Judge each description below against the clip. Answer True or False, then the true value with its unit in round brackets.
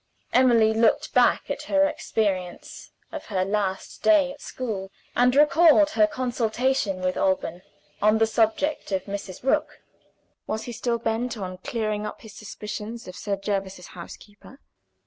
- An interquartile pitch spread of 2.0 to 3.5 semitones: False (4.2 semitones)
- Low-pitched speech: False (220 Hz)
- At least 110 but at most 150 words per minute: True (145 wpm)